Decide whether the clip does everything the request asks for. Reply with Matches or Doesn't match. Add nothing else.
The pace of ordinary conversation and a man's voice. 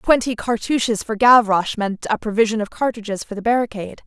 Doesn't match